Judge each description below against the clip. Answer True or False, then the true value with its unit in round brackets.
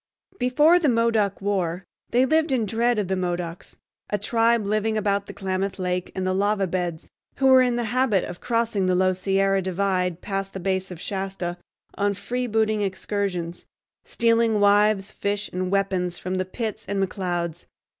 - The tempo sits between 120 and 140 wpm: False (170 wpm)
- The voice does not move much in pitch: False (3.2 semitones)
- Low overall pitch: False (200 Hz)